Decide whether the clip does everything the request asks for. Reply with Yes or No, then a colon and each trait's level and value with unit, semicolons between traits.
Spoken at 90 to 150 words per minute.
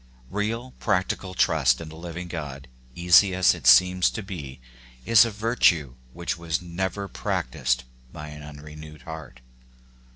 Yes: average, 140 wpm